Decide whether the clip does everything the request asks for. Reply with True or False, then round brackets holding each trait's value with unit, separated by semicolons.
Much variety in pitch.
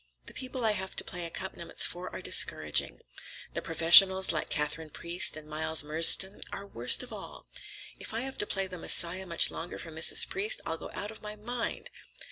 False (4.4 semitones)